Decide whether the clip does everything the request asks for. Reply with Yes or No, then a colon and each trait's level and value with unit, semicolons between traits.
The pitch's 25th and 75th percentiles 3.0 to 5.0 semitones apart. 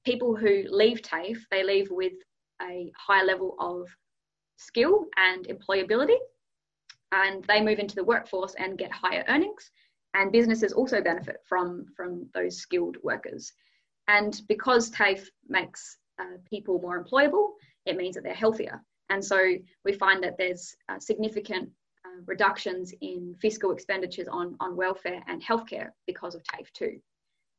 Yes: average, 3.5 semitones